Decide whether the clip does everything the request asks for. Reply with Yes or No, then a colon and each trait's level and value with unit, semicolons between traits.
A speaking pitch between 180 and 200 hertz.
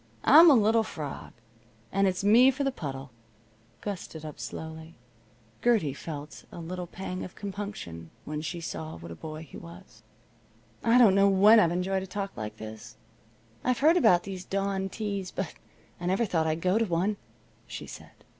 Yes: medium, 185 Hz